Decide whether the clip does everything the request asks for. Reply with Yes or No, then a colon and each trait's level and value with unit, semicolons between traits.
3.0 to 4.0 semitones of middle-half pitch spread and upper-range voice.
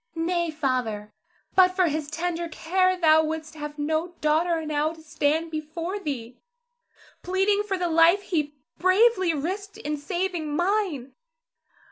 Yes: average, 3.3 semitones; very high, 325 Hz